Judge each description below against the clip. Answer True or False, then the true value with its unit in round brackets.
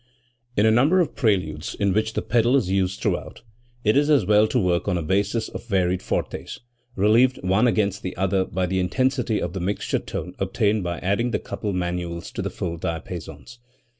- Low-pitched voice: True (100 Hz)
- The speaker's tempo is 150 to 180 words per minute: False (195 wpm)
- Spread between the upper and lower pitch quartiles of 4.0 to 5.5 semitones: False (3.6 semitones)